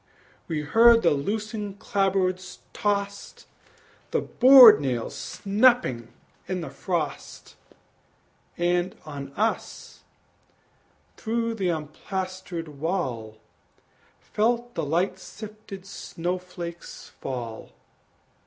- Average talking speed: No, slow, 90 wpm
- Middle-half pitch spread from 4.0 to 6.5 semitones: Yes, average, 5.0 semitones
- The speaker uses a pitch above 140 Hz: Yes, medium, 185 Hz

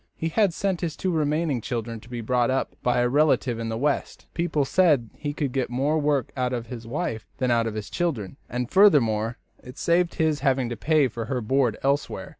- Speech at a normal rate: No, fast, 220 wpm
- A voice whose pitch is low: Yes, low, 130 Hz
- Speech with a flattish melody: No, average, 4.6 semitones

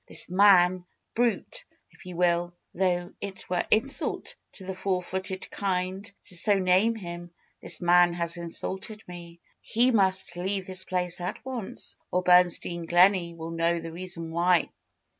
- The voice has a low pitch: No, medium, 180 Hz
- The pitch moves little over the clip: Yes, narrow, 1.7 semitones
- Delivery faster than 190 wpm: No, average, 160 wpm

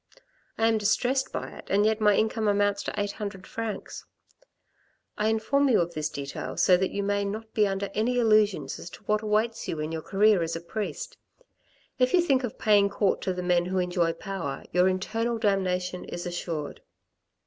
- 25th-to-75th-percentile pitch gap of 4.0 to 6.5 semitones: No, average, 3.3 semitones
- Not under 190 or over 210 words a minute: Yes, average, 195 wpm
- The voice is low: No, high, 205 Hz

